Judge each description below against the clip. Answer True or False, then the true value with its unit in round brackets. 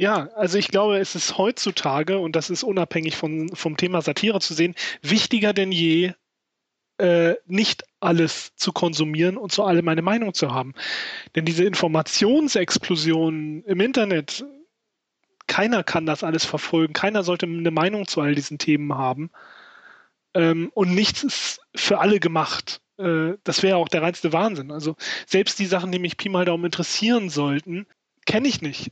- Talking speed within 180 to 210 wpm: False (165 wpm)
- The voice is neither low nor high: True (175 Hz)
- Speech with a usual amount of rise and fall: True (3.5 semitones)